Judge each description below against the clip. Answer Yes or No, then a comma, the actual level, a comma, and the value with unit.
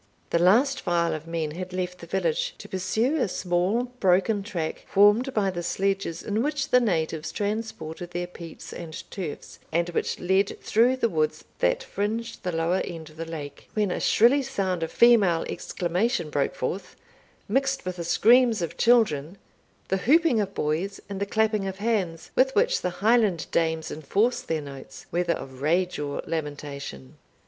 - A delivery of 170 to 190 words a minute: Yes, average, 175 wpm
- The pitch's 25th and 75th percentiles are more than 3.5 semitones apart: Yes, average, 5.1 semitones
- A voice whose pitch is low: No, medium, 185 Hz